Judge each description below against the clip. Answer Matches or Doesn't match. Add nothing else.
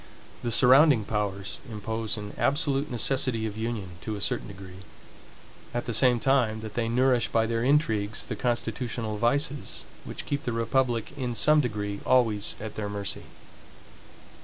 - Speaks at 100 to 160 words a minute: Matches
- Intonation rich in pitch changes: Doesn't match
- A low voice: Matches